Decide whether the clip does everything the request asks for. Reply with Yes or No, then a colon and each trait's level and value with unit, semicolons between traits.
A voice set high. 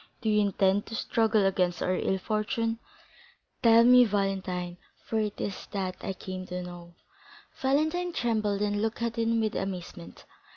Yes: high, 205 Hz